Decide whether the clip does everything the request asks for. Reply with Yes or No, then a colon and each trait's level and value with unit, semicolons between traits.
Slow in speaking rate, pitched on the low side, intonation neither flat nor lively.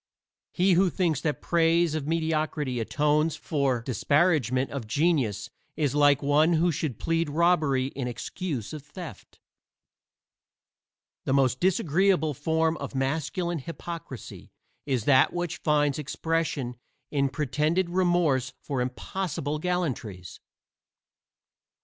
No: slow, 115 wpm; medium, 150 Hz; average, 3.8 semitones